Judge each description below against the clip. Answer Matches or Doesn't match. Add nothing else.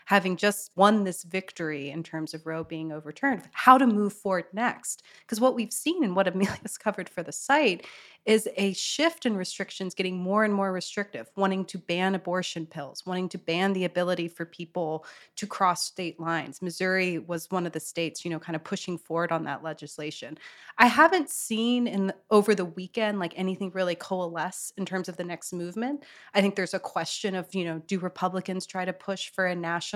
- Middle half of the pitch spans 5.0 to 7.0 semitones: Doesn't match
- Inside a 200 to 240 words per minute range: Matches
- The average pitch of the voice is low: Doesn't match